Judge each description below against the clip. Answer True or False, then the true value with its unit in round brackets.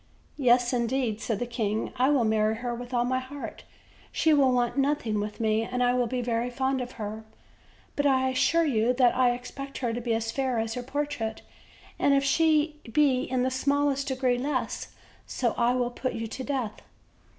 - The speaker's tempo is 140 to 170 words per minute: False (200 wpm)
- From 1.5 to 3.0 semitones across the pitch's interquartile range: True (2.5 semitones)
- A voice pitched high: True (250 Hz)